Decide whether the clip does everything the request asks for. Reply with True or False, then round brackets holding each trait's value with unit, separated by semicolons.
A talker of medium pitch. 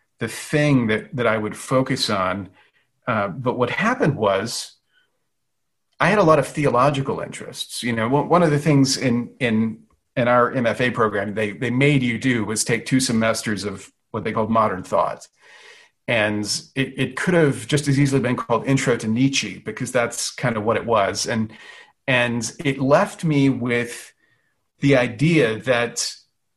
False (125 Hz)